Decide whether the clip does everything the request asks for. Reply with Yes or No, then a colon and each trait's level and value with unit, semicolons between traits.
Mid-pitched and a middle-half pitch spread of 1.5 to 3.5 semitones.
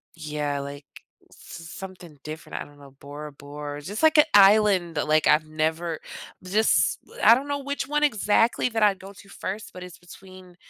No: medium, 180 Hz; wide, 5.6 semitones